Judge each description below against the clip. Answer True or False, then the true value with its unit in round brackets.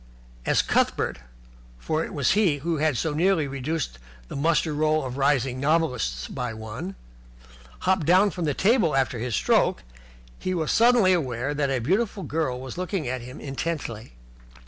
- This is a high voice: False (150 Hz)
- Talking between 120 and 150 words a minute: False (165 wpm)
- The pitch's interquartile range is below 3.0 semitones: False (4.8 semitones)